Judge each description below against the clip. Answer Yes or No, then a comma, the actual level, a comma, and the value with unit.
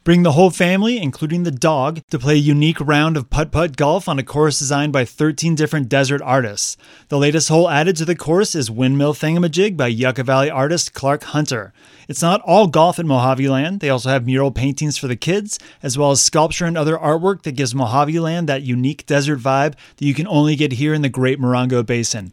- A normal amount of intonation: Yes, average, 3.2 semitones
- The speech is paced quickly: Yes, fast, 220 wpm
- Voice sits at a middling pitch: Yes, medium, 150 Hz